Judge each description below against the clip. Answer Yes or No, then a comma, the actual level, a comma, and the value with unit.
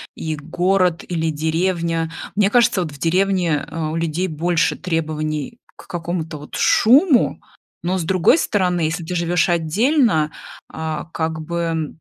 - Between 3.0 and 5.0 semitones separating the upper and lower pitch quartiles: No, narrow, 2.5 semitones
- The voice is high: No, medium, 170 Hz